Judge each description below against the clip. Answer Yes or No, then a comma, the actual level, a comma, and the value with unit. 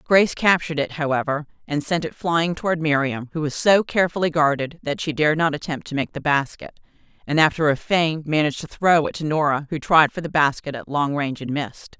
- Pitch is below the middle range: No, medium, 155 Hz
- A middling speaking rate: No, fast, 220 wpm